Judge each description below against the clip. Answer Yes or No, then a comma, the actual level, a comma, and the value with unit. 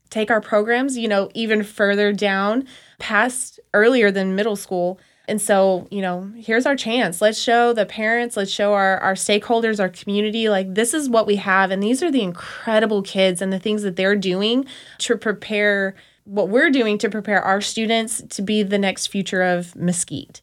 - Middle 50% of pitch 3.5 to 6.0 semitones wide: No, average, 2.7 semitones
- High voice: Yes, high, 210 Hz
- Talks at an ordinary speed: Yes, average, 190 wpm